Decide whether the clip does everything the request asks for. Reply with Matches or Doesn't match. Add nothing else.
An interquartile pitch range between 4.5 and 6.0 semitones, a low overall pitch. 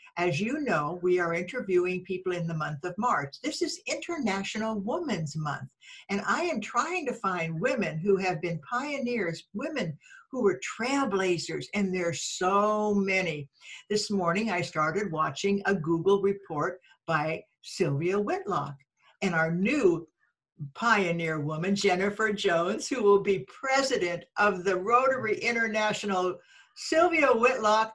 Doesn't match